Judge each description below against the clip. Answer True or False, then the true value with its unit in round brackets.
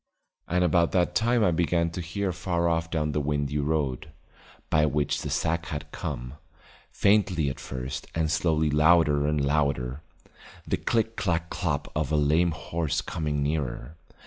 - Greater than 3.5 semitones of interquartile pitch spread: False (2.7 semitones)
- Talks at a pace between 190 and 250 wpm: False (160 wpm)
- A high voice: False (80 Hz)